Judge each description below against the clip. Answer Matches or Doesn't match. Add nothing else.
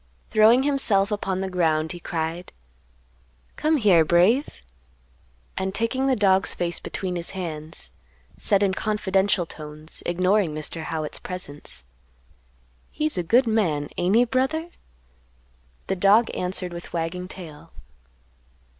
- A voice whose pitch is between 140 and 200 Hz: Matches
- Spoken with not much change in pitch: Doesn't match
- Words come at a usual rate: Doesn't match